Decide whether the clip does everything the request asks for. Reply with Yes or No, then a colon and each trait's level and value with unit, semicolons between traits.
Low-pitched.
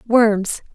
No: high, 220 Hz